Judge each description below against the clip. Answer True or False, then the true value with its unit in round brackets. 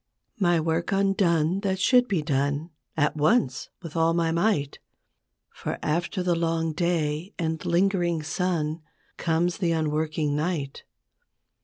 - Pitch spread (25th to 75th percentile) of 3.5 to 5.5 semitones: False (2.6 semitones)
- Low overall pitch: False (165 Hz)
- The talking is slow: True (130 wpm)